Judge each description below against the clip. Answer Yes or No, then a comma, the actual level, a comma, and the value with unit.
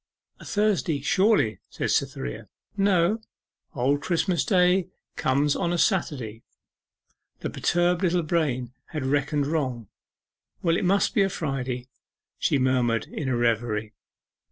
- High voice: No, medium, 150 Hz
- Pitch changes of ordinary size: No, wide, 6.1 semitones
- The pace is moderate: No, slow, 130 wpm